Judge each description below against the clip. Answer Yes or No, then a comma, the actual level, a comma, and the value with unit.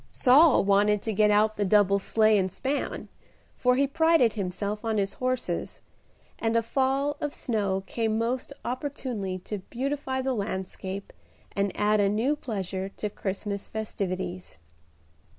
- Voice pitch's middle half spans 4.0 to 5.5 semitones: Yes, average, 4.4 semitones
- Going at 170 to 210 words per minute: No, average, 145 wpm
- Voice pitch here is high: Yes, high, 215 Hz